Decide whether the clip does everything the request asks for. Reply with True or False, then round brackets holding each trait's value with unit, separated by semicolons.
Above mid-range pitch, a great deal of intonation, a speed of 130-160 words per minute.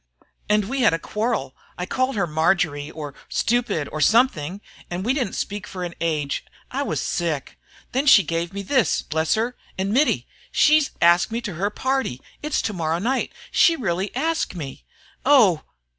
False (195 Hz; 7.1 semitones; 175 wpm)